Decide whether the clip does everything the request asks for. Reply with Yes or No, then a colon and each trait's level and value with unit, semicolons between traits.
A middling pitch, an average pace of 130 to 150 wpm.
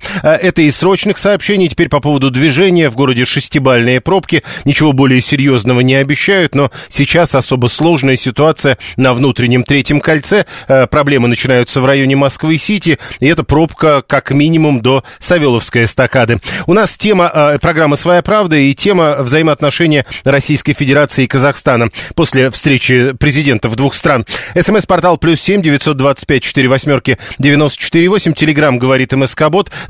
Yes: medium, 145 Hz; average, 145 wpm